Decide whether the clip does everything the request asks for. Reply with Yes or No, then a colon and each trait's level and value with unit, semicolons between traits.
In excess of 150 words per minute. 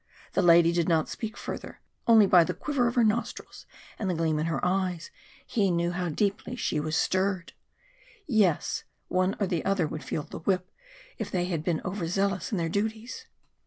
Yes: average, 195 wpm